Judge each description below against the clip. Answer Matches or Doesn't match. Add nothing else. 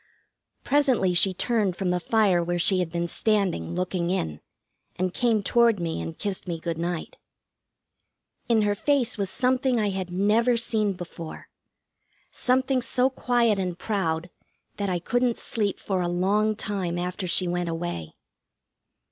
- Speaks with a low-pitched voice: Doesn't match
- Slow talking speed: Doesn't match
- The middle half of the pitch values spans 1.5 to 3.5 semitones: Doesn't match